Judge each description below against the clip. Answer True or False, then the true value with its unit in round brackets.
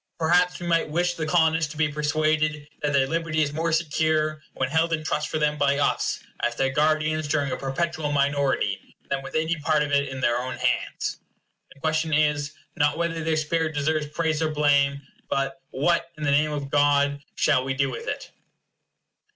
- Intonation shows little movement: True (1.9 semitones)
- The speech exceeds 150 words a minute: True (195 wpm)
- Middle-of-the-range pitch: True (150 Hz)